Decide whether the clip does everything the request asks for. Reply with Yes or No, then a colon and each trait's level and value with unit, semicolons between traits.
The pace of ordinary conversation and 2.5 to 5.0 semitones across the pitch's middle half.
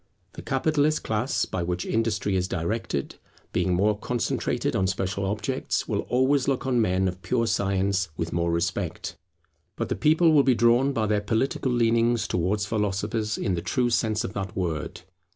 Yes: average, 170 wpm; average, 4.4 semitones